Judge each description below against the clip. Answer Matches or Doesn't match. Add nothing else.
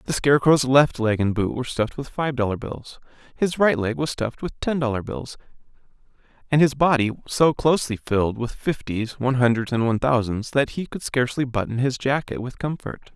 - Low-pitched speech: Matches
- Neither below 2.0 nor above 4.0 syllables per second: Doesn't match